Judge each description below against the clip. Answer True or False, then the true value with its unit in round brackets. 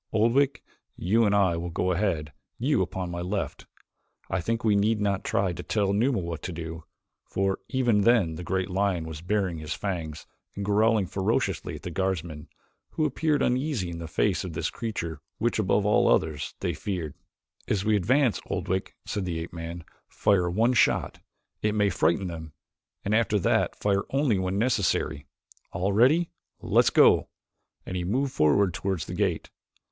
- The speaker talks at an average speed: True (175 wpm)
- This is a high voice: False (95 Hz)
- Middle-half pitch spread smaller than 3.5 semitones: False (3.9 semitones)